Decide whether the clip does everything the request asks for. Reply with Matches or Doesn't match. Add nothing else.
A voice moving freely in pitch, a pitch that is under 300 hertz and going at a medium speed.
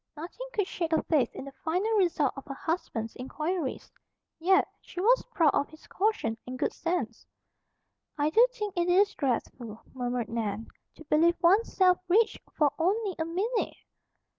Doesn't match